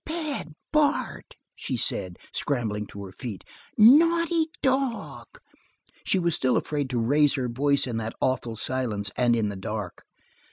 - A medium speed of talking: Yes, average, 150 wpm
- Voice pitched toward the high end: No, low, 130 Hz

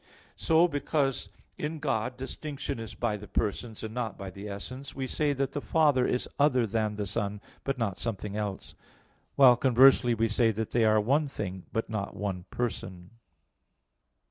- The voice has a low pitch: Yes, low, 115 Hz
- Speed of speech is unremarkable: Yes, average, 170 wpm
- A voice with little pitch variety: No, average, 4.5 semitones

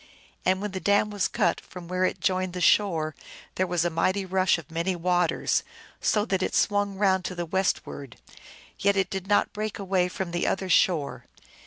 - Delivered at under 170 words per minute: No, average, 195 wpm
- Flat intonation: Yes, narrow, 1.9 semitones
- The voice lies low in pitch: No, medium, 185 Hz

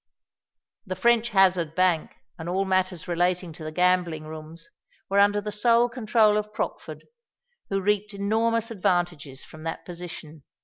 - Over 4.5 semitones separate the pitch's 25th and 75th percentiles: No, average, 3.8 semitones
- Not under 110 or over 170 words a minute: Yes, average, 145 wpm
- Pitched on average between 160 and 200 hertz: Yes, medium, 185 Hz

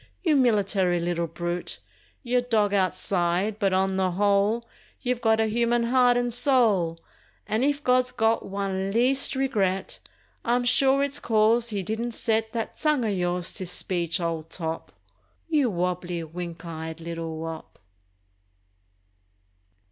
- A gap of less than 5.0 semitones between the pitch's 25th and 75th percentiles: No, wide, 5.4 semitones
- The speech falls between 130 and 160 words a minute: Yes, average, 140 wpm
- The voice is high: Yes, high, 205 Hz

